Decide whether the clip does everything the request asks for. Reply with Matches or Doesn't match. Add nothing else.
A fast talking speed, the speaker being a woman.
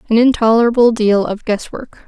Doesn't match